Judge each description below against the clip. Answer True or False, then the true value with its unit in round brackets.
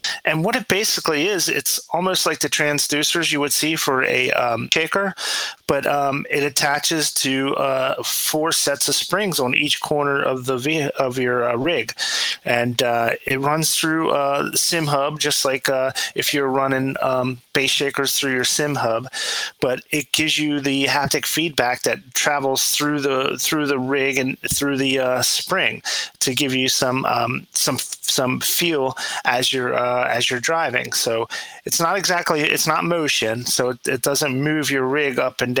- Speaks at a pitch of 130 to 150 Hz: True (140 Hz)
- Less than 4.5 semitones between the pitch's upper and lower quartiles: True (2.5 semitones)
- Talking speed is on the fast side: False (185 wpm)